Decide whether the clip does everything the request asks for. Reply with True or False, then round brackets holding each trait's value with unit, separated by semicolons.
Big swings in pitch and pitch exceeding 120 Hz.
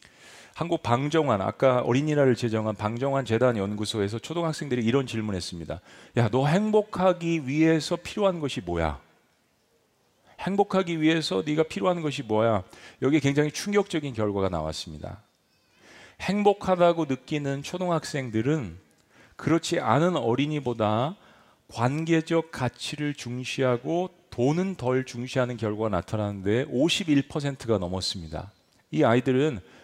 True (6.6 semitones; 135 Hz)